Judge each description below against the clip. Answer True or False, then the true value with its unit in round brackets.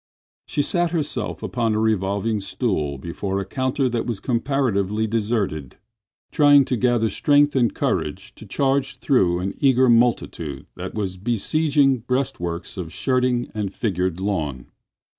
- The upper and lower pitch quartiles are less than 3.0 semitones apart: False (5.4 semitones)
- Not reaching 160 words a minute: True (140 wpm)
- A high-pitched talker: False (115 Hz)